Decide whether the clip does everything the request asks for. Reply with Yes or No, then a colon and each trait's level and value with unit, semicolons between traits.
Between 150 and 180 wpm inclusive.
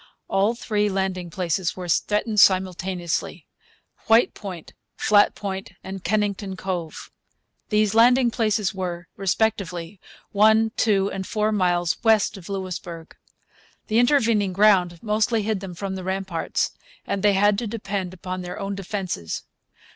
No: slow, 135 wpm